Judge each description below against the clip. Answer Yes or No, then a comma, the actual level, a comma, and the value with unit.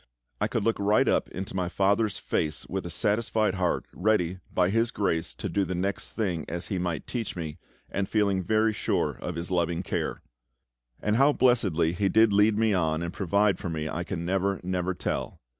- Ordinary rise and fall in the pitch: Yes, average, 3.3 semitones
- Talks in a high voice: No, very low, 95 Hz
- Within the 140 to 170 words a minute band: No, average, 200 wpm